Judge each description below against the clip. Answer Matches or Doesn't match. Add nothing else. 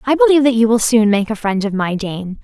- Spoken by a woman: Matches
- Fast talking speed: Matches